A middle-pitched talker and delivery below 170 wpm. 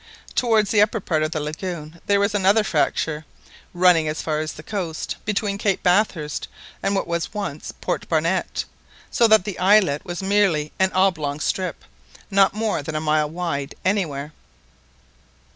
Yes: medium, 180 Hz; average, 160 wpm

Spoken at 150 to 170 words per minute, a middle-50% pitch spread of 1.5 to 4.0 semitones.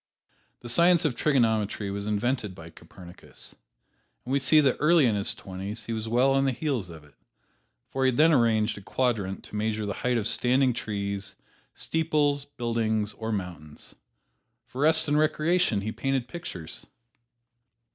No: average, 165 wpm; average, 5.3 semitones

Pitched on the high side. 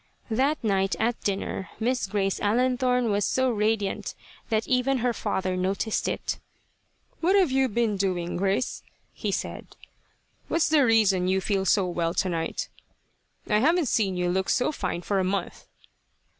Yes: high, 210 Hz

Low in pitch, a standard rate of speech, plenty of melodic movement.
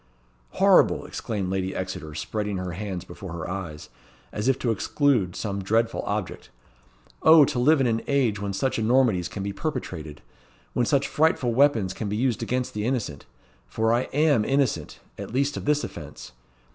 Yes: low, 110 Hz; average, 170 wpm; wide, 5.9 semitones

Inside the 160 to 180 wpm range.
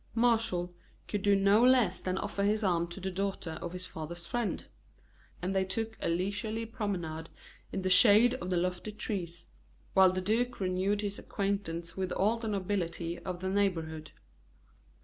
Yes: average, 170 wpm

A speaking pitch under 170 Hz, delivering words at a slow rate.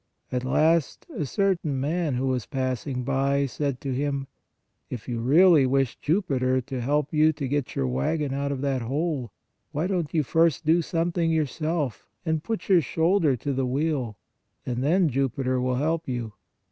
No: medium, 140 Hz; average, 180 wpm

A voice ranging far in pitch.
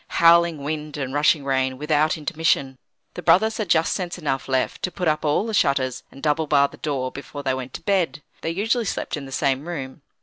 No: average, 3.7 semitones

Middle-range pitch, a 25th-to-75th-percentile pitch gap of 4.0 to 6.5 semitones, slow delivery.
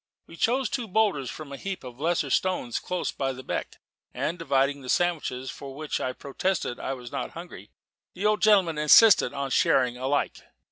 No: medium, 150 Hz; wide, 5.5 semitones; average, 190 wpm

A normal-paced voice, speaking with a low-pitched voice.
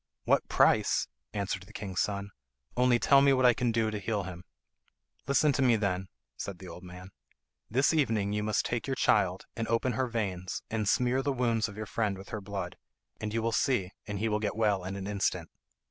No: fast, 210 wpm; low, 110 Hz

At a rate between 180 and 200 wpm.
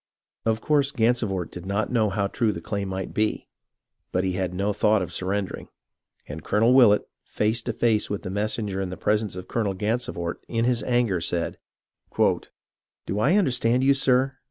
Yes: average, 190 wpm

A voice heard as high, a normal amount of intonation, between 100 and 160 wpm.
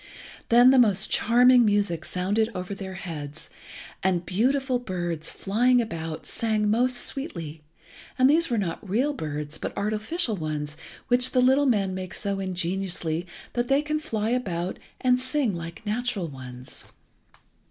No: high, 205 Hz; wide, 6.2 semitones; average, 145 wpm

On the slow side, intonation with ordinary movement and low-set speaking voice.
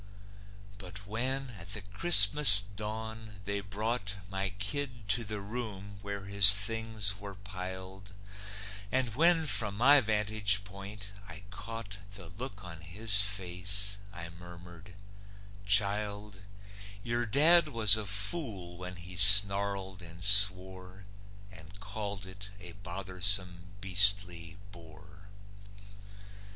No: slow, 115 wpm; narrow, 2.1 semitones; low, 100 Hz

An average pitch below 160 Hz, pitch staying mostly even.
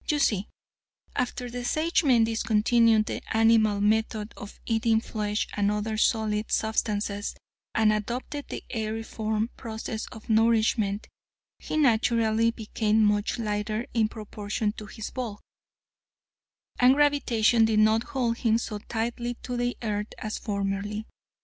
No: high, 220 Hz; narrow, 1.8 semitones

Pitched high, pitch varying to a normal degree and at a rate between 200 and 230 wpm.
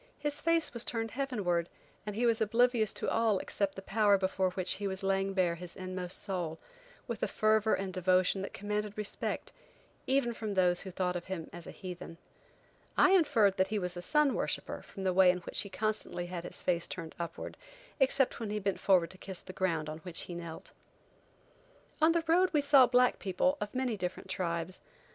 Yes: high, 195 Hz; average, 3.9 semitones; fast, 205 wpm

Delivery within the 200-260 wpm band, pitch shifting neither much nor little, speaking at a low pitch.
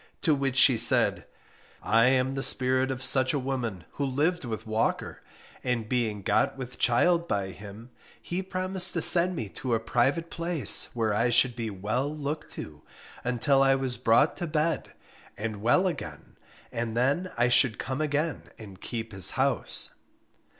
No: average, 170 wpm; average, 4.5 semitones; low, 130 Hz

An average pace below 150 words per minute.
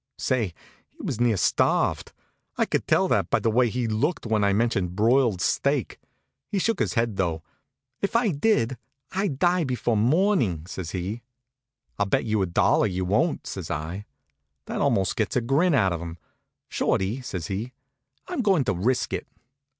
No: average, 175 wpm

